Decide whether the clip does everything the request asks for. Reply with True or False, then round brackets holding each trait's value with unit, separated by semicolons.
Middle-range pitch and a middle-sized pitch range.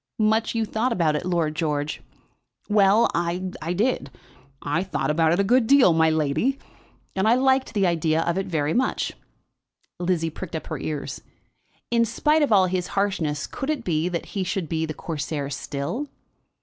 False (180 Hz; 5.7 semitones)